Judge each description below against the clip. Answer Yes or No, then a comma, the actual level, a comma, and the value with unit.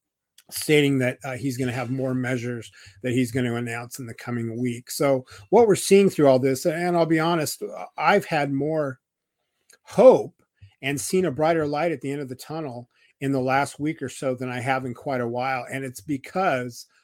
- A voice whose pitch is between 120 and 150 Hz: Yes, low, 135 Hz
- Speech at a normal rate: No, fast, 210 wpm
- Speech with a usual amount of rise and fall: Yes, average, 3.2 semitones